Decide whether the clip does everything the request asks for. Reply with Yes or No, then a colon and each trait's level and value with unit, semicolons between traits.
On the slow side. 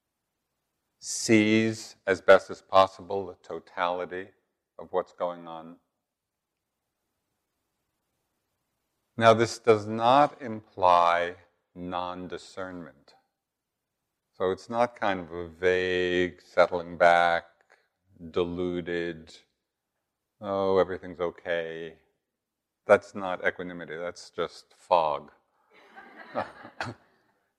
Yes: slow, 80 wpm